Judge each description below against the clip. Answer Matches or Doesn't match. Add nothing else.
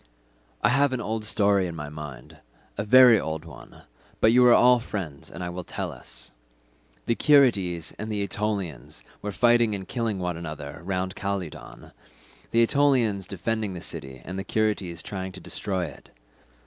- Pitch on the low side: Matches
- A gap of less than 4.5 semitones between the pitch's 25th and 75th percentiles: Doesn't match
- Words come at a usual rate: Matches